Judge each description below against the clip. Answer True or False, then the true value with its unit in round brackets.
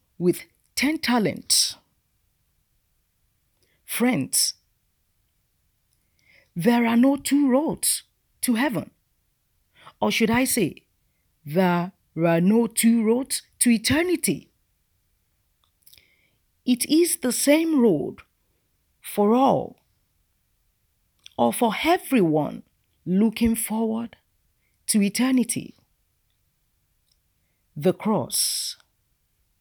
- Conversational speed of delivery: False (75 wpm)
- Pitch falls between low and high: False (215 Hz)